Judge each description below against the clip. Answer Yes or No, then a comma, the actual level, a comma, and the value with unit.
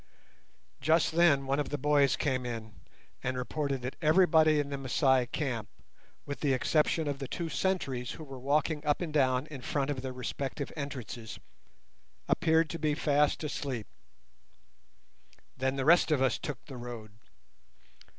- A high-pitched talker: No, medium, 140 Hz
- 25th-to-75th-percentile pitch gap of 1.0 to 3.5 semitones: Yes, average, 3.0 semitones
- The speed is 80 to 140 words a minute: No, average, 160 wpm